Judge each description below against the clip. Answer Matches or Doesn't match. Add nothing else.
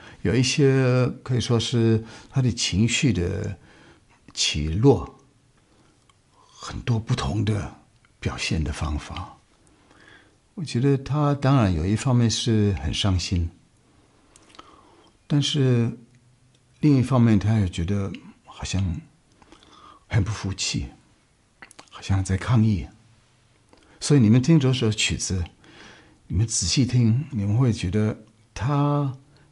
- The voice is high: Doesn't match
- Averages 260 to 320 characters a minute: Doesn't match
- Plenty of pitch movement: Doesn't match